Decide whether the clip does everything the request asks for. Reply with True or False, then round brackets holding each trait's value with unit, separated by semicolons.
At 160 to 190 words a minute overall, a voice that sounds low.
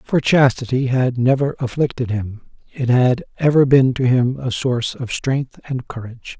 True (170 wpm; 125 Hz)